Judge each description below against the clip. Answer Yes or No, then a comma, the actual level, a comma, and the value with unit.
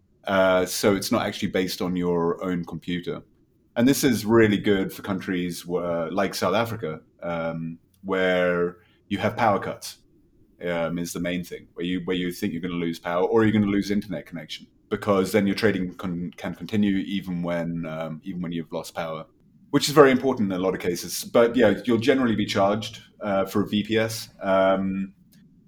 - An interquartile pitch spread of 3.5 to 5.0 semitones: No, average, 2.8 semitones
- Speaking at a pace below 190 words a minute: No, average, 195 wpm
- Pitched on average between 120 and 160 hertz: No, very low, 95 Hz